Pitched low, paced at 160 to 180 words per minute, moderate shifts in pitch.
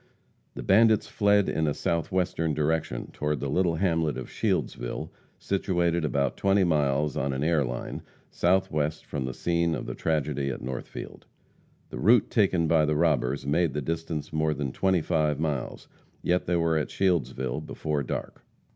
Yes: very low, 80 Hz; average, 165 wpm; average, 3.3 semitones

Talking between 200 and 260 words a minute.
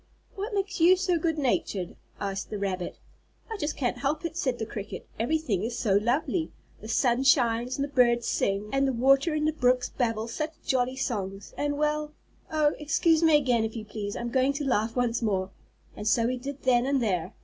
Yes: fast, 205 wpm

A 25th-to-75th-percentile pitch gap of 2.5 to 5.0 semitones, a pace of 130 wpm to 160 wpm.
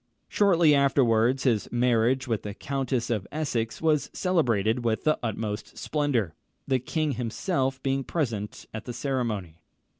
Yes: average, 3.9 semitones; average, 140 wpm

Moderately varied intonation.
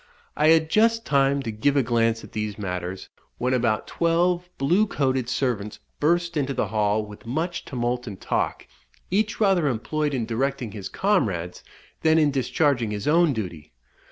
No: wide, 6.7 semitones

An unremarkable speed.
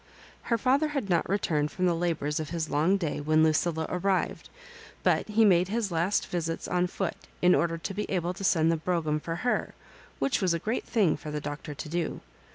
No: fast, 210 wpm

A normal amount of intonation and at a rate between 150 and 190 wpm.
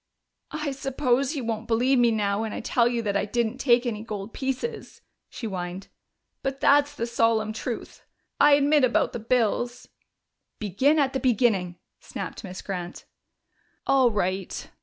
Yes: average, 4.1 semitones; average, 160 wpm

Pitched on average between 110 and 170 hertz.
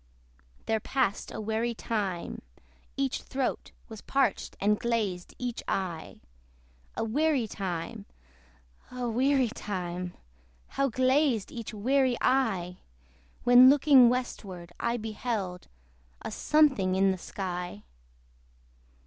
No: high, 225 Hz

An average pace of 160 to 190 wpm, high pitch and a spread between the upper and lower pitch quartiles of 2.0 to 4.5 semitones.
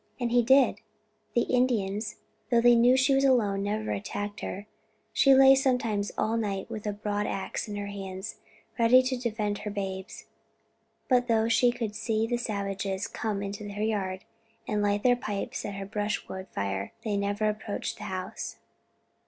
Yes: average, 170 wpm; high, 210 Hz; average, 2.9 semitones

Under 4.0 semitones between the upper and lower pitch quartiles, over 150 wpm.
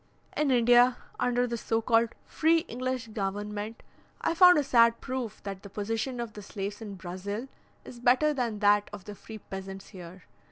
Yes: average, 3.5 semitones; average, 175 wpm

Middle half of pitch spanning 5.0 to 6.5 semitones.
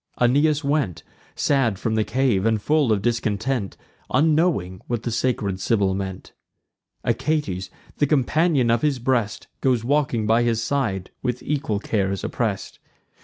Yes: average, 5.3 semitones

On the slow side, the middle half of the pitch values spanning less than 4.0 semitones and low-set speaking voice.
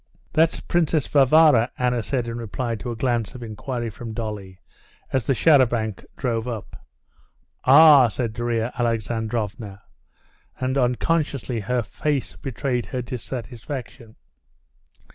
Yes: slow, 125 wpm; average, 2.7 semitones; low, 120 Hz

